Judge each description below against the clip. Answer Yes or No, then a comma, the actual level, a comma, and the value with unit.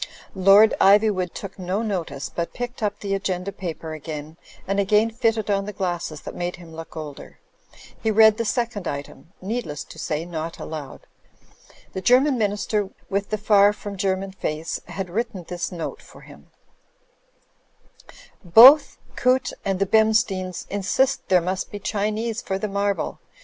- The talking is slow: No, average, 160 wpm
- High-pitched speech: Yes, high, 195 Hz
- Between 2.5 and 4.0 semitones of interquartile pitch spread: Yes, average, 3.6 semitones